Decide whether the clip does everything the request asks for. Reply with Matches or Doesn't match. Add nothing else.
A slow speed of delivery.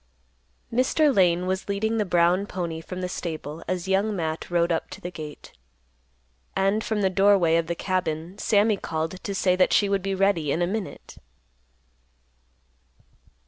Doesn't match